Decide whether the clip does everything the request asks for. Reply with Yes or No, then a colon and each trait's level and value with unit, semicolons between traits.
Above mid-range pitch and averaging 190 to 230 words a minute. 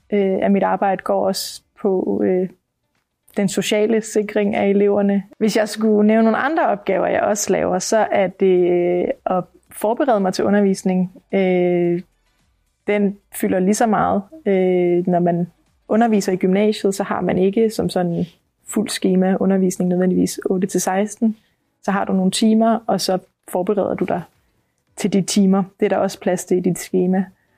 No: high, 195 Hz; average, 170 wpm